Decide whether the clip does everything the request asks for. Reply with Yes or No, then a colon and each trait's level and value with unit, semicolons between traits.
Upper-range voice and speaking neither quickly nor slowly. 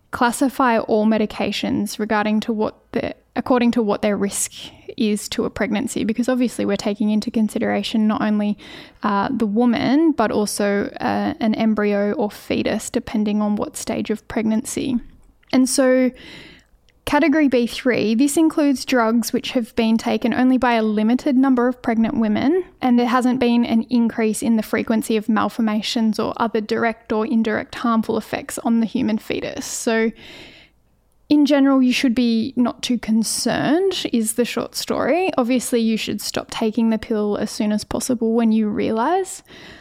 Yes: high, 230 Hz; average, 165 wpm